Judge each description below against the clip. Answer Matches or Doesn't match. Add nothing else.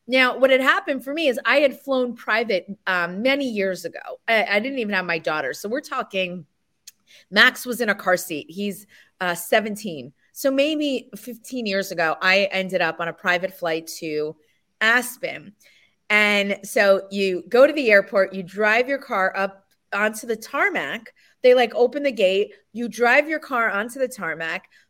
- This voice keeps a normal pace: Matches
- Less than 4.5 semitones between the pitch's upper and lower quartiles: Doesn't match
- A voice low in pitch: Doesn't match